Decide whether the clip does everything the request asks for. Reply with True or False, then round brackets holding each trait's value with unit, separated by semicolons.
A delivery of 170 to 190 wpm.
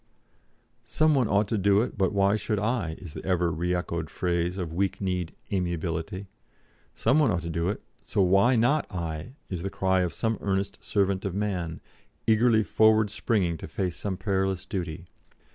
True (180 wpm)